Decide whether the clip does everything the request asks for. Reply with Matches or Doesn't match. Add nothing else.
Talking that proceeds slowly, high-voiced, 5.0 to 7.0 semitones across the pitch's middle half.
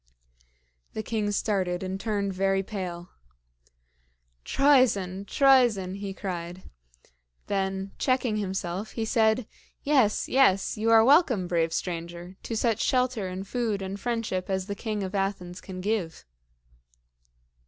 Doesn't match